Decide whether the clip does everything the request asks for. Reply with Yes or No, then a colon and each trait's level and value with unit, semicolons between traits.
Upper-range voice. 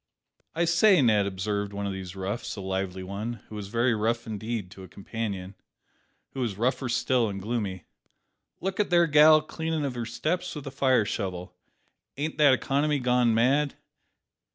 No: low, 115 Hz